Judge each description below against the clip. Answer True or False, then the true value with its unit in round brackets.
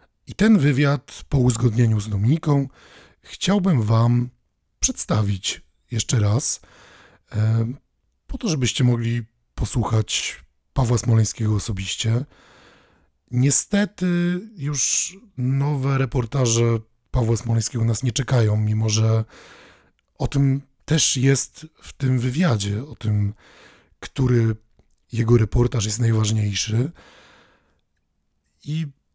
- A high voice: False (120 Hz)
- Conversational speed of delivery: False (95 wpm)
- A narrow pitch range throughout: False (3.9 semitones)